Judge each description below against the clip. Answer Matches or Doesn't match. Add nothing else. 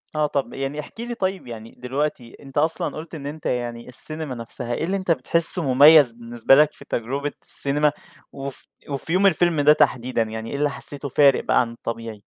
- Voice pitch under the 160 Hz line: Matches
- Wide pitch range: Doesn't match